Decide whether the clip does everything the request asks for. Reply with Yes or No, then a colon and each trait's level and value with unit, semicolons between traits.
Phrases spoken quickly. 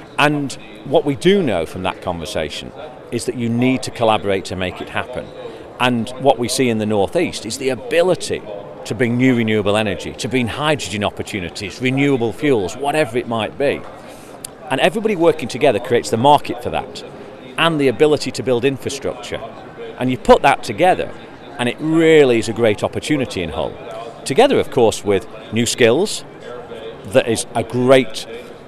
No: average, 170 wpm